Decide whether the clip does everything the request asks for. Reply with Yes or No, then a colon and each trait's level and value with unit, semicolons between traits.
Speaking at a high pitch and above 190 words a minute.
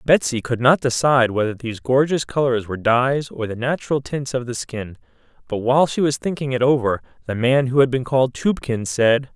No: low, 125 Hz; fast, 205 wpm